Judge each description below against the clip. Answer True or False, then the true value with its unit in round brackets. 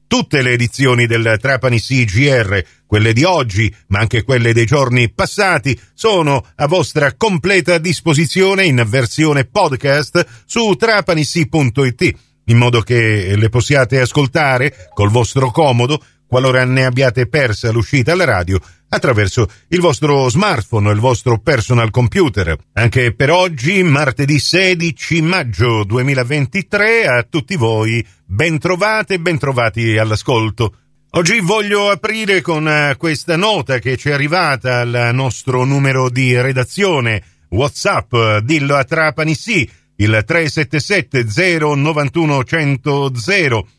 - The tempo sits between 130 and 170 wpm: False (120 wpm)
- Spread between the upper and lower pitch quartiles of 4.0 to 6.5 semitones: True (5.5 semitones)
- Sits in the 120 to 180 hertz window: True (135 Hz)